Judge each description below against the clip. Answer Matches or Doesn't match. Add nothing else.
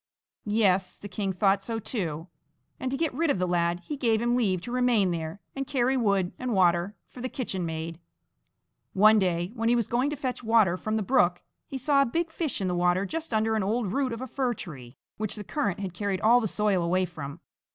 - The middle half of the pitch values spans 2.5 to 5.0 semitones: Doesn't match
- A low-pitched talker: Doesn't match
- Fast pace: Matches